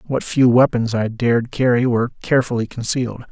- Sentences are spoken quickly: No, average, 165 wpm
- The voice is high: No, low, 120 Hz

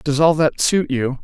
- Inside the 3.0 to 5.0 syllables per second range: Yes, 4.2 syllables/s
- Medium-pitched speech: Yes, medium, 145 Hz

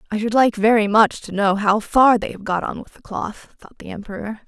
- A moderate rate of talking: No, fast, 255 wpm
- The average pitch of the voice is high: Yes, high, 215 Hz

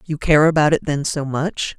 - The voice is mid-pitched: Yes, medium, 150 Hz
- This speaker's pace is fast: Yes, fast, 235 wpm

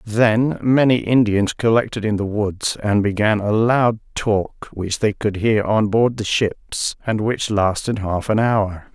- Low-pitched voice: Yes, low, 105 Hz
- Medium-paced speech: Yes, average, 175 wpm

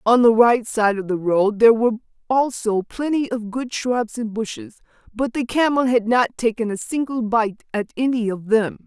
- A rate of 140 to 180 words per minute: No, average, 195 wpm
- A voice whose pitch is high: Yes, high, 230 Hz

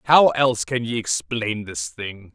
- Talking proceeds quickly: No, average, 180 wpm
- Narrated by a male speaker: Yes, male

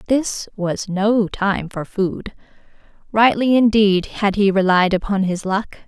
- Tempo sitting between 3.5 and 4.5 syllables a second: Yes, 3.9 syllables/s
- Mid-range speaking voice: No, high, 200 Hz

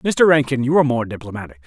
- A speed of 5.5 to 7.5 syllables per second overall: Yes, 6.9 syllables/s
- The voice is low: Yes, low, 130 Hz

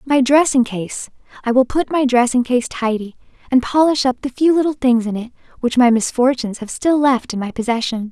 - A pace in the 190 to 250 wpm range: Yes, average, 200 wpm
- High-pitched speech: Yes, very high, 255 Hz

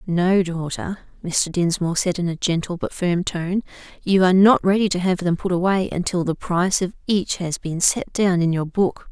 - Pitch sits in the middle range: Yes, medium, 180 Hz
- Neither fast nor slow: No, fast, 210 wpm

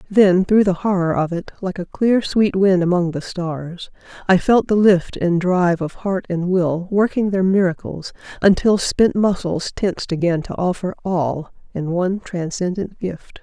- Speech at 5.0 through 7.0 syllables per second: No, 4.4 syllables/s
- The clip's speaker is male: No, female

